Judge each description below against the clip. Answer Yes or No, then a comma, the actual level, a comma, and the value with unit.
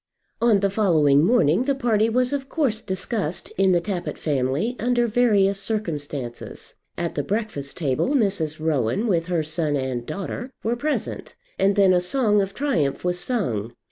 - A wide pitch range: Yes, wide, 6.9 semitones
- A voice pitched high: Yes, high, 195 Hz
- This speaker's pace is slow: No, average, 165 wpm